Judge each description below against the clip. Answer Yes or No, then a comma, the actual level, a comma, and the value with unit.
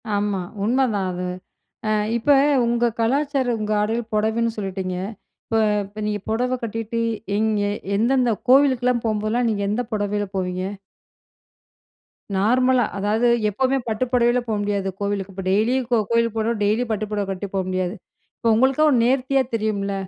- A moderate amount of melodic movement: Yes, average, 3.1 semitones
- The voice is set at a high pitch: Yes, high, 220 Hz